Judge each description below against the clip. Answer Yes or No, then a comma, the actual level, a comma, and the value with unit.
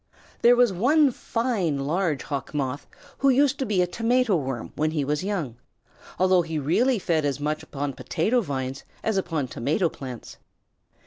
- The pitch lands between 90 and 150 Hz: No, medium, 165 Hz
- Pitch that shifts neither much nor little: No, wide, 8.1 semitones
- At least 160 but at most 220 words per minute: Yes, average, 170 wpm